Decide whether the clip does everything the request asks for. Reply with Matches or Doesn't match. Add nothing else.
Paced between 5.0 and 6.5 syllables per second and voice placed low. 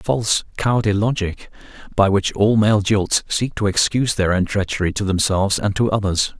Matches